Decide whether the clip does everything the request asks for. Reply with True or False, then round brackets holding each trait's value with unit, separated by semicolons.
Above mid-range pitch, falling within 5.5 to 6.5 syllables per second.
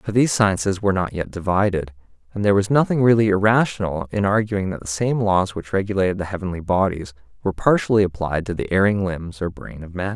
False (95 Hz; 6.0 syllables/s)